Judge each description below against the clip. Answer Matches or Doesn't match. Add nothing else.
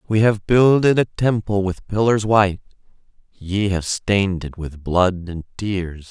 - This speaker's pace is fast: Doesn't match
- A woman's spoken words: Doesn't match